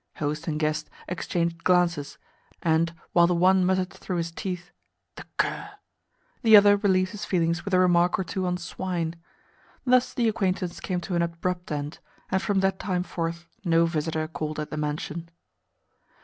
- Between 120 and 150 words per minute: No, average, 170 wpm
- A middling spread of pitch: No, narrow, 2.1 semitones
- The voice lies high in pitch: No, medium, 175 Hz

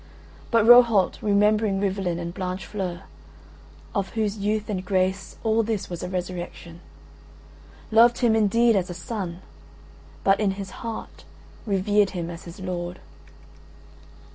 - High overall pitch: Yes, high, 195 Hz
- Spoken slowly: Yes, slow, 130 wpm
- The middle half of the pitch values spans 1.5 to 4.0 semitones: Yes, average, 2.9 semitones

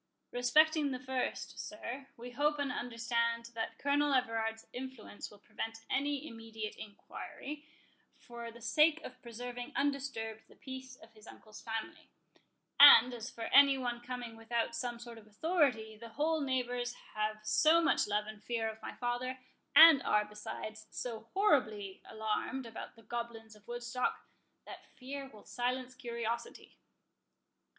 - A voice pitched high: Yes, high, 240 Hz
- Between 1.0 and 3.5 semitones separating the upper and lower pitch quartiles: Yes, average, 3.0 semitones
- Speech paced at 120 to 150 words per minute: Yes, average, 145 wpm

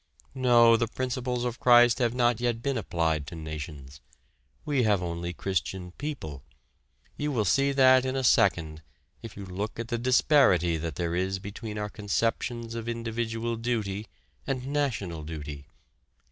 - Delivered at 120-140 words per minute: No, average, 155 wpm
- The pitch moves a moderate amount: No, wide, 5.9 semitones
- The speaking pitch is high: No, low, 115 Hz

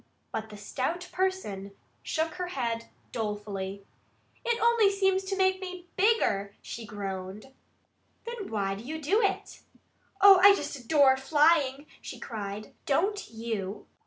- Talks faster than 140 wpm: No, slow, 135 wpm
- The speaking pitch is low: No, very high, 280 Hz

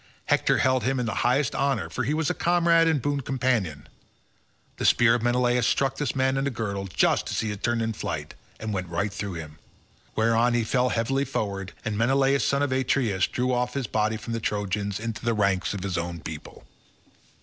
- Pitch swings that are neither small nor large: Yes, average, 4.5 semitones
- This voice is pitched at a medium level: No, low, 115 Hz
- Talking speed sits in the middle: No, fast, 210 wpm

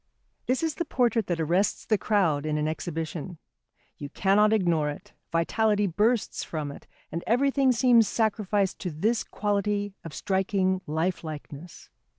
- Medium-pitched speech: No, high, 195 Hz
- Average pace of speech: Yes, average, 145 wpm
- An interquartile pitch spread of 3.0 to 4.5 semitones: No, average, 4.9 semitones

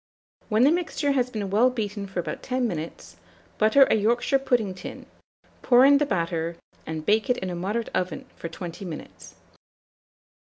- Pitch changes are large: Yes, wide, 5.9 semitones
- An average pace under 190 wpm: Yes, average, 170 wpm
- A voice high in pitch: Yes, high, 215 Hz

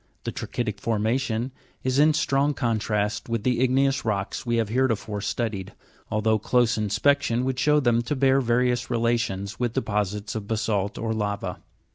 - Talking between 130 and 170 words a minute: Yes, average, 160 wpm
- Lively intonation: No, average, 3.5 semitones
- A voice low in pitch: Yes, low, 115 Hz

